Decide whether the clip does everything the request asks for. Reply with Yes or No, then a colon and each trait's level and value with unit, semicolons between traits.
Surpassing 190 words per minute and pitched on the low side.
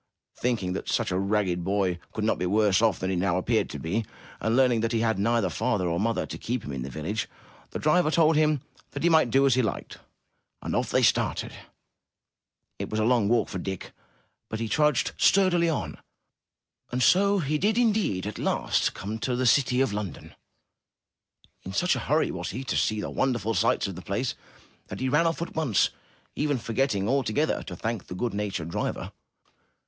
Yes: fast, 205 wpm; low, 115 Hz